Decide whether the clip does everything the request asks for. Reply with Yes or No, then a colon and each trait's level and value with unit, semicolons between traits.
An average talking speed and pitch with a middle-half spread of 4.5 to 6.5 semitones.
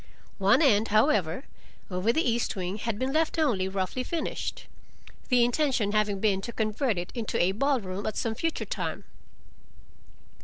Yes: average, 160 wpm; average, 4.9 semitones